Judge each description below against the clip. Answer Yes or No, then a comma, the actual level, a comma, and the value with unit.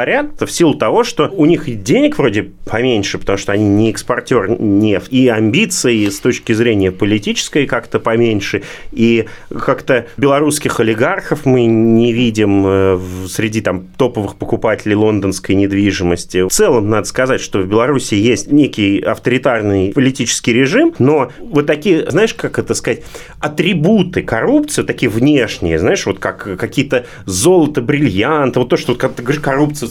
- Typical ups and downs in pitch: No, wide, 5.8 semitones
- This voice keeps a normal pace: Yes, average, 140 wpm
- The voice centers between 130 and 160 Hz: No, low, 115 Hz